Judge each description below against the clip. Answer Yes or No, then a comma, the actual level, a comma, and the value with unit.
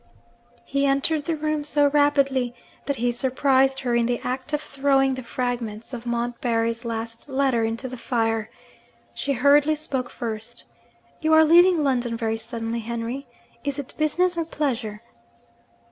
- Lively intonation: No, average, 3.5 semitones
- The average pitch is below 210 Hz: No, very high, 260 Hz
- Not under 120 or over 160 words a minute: Yes, average, 150 wpm